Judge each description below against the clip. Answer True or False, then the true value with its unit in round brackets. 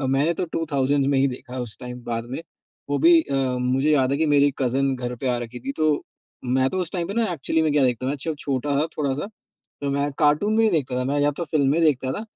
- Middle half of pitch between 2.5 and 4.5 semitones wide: True (3.3 semitones)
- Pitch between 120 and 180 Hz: True (140 Hz)